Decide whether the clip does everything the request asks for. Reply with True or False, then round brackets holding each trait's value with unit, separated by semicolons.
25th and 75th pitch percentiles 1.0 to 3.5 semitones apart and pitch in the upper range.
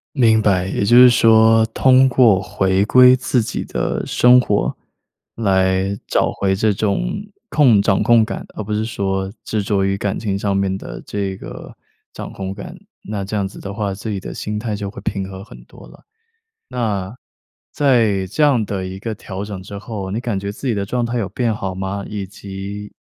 False (2.8 semitones; 105 Hz)